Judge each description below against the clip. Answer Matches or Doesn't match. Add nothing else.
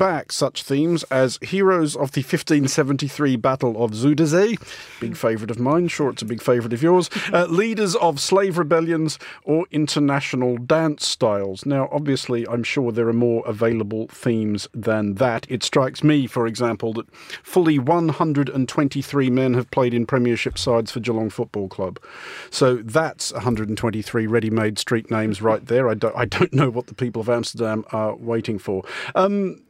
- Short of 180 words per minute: Matches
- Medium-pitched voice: Doesn't match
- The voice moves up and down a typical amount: Matches